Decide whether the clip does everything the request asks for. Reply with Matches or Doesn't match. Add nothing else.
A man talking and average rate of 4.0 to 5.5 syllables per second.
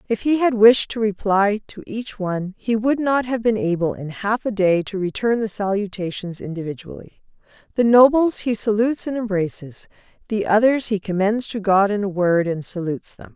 Doesn't match